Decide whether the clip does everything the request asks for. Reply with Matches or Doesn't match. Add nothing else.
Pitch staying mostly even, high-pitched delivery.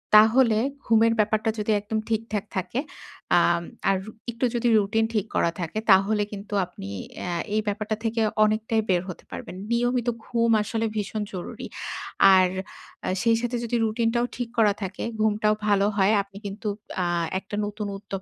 Matches